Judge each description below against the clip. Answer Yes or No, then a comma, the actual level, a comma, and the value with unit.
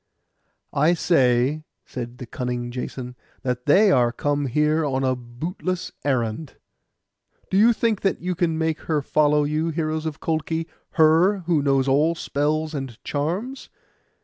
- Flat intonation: No, average, 3.8 semitones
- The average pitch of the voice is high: No, medium, 150 Hz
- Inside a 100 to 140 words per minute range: No, average, 150 wpm